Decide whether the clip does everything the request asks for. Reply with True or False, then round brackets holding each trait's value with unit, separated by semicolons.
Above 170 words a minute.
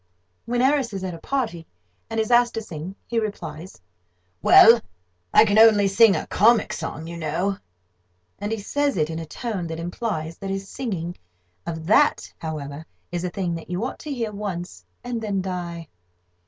True (180 wpm)